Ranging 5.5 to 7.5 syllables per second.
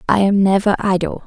Yes: 5.7 syllables/s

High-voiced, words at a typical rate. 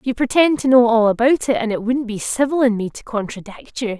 No: high, 240 Hz; fast, 255 wpm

